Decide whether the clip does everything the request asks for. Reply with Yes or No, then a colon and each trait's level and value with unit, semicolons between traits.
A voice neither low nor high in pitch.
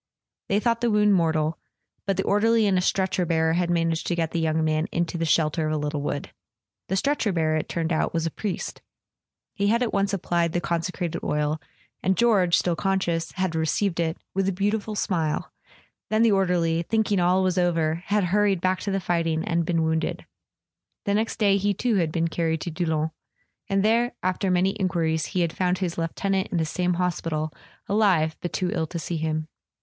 Yes: medium, 175 Hz